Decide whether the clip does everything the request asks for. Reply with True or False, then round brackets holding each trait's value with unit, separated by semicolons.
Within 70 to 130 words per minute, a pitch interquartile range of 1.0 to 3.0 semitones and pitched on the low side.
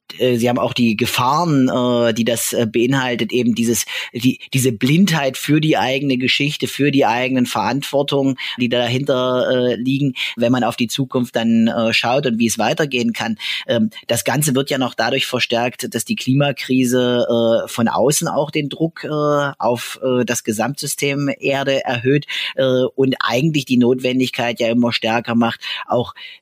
False (150 wpm; 2.5 semitones; 125 Hz)